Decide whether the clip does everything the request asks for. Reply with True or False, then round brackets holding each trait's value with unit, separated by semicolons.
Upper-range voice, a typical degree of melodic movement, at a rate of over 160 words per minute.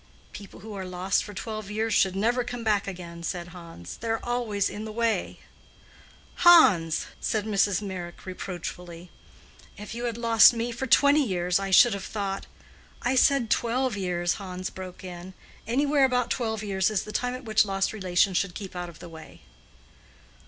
True (200 Hz; 4.1 semitones; 180 wpm)